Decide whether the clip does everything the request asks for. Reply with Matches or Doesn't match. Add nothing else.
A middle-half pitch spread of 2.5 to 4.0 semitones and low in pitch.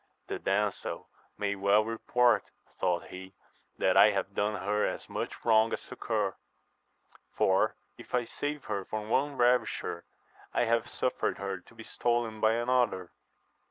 Matches